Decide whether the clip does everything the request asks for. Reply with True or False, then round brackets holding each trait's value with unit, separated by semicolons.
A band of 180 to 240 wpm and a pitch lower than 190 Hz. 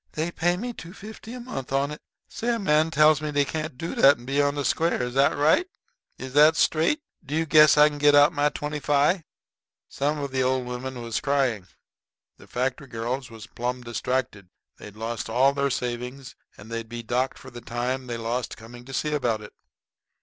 True (200 wpm; 135 Hz)